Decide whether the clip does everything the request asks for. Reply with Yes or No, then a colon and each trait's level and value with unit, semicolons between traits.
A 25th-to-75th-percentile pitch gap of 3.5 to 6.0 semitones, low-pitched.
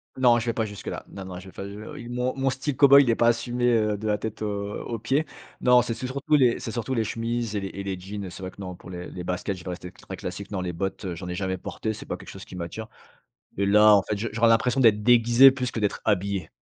Yes: average, 3.8 semitones; low, 110 Hz